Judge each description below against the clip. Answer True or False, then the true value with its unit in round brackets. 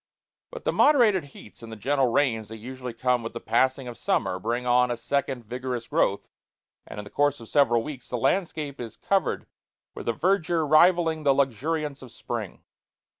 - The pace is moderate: True (185 wpm)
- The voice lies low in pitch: True (130 Hz)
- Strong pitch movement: False (4.3 semitones)